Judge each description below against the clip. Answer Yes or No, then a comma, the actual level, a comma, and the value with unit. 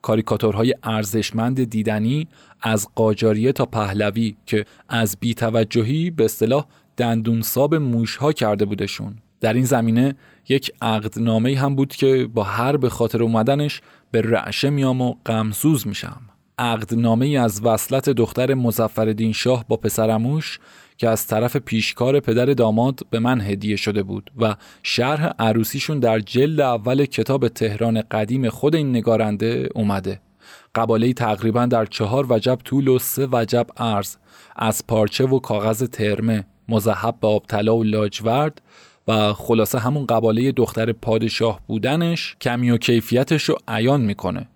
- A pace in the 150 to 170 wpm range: No, average, 135 wpm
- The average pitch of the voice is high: No, low, 115 Hz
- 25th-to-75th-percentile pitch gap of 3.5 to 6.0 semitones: No, average, 2.8 semitones